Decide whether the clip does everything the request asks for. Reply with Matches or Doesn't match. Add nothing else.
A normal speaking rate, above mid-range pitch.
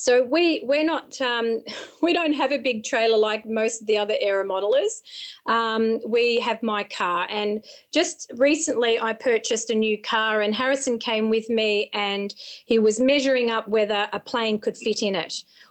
Matches